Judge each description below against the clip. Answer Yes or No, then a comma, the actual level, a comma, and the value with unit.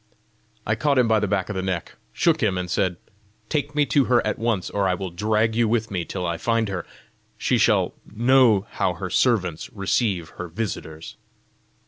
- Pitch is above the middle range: No, low, 105 Hz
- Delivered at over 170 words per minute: Yes, average, 195 wpm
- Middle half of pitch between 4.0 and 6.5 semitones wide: Yes, average, 4.3 semitones